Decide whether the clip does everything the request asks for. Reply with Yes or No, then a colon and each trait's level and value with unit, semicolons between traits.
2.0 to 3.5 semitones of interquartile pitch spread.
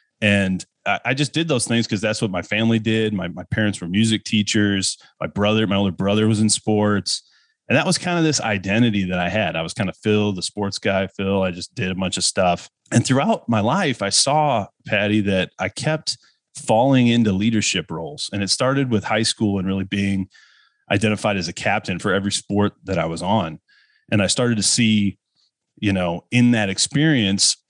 Yes: average, 2.9 semitones